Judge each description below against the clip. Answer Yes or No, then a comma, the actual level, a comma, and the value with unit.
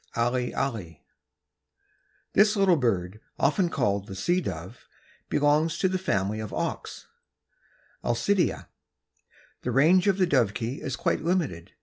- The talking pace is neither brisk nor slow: No, slow, 125 wpm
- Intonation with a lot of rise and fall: Yes, wide, 8.9 semitones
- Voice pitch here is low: Yes, low, 130 Hz